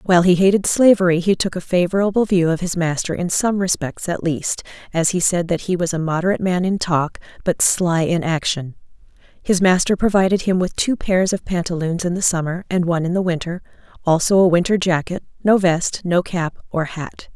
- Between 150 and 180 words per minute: No, fast, 205 wpm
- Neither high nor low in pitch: Yes, medium, 175 Hz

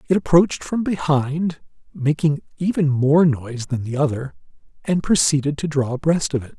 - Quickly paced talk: No, average, 165 wpm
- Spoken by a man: Yes, male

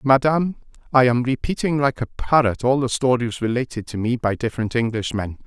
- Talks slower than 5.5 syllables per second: No, 5.7 syllables/s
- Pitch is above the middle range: No, low, 125 Hz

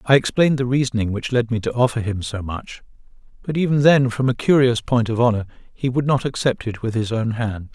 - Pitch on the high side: No, low, 120 Hz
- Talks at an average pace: No, fast, 235 wpm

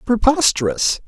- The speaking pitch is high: Yes, high, 195 Hz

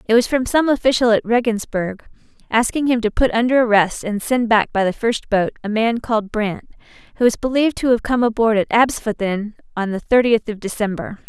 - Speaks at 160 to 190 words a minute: No, average, 200 wpm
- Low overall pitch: No, high, 225 Hz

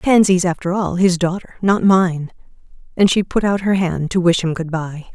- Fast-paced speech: No, average, 185 wpm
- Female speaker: Yes, female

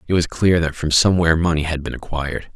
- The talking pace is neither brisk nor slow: No, fast, 235 wpm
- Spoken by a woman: No, male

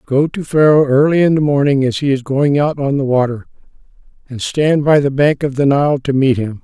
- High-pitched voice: No, medium, 140 Hz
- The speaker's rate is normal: No, fast, 235 wpm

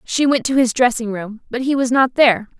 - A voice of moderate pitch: No, high, 245 Hz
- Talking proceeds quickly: Yes, fast, 255 wpm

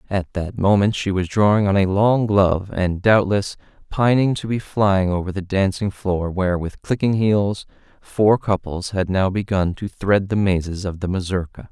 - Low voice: Yes, very low, 95 Hz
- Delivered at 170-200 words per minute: Yes, average, 185 wpm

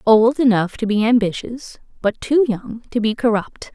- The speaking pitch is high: Yes, high, 225 Hz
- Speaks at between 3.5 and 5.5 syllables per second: Yes, 4.5 syllables/s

